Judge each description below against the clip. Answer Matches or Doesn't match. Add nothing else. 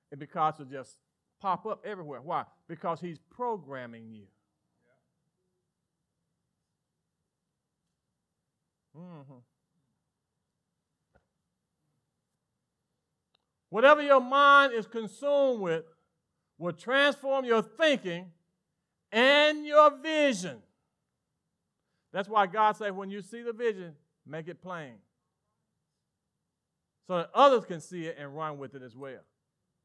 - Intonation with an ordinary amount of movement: Doesn't match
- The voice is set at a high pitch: Doesn't match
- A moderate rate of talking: Doesn't match